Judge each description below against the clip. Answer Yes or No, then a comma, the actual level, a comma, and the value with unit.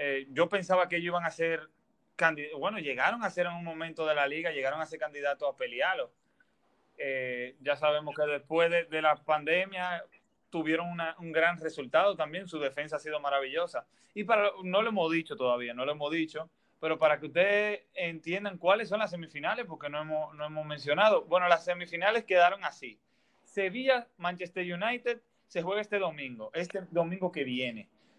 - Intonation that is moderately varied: Yes, average, 3.7 semitones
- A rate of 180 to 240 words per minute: Yes, average, 185 wpm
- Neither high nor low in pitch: Yes, medium, 165 Hz